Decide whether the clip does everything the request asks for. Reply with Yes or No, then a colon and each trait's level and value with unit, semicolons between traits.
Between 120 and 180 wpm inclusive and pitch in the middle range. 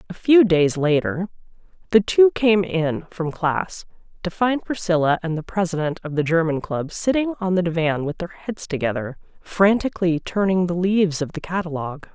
Yes: average, 175 wpm; medium, 175 Hz